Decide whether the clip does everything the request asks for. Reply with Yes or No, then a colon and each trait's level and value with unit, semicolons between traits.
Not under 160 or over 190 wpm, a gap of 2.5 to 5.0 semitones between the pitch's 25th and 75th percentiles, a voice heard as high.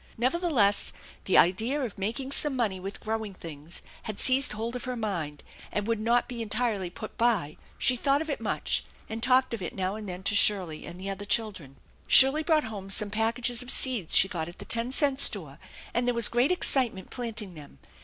No: fast, 205 wpm; average, 4.5 semitones; high, 220 Hz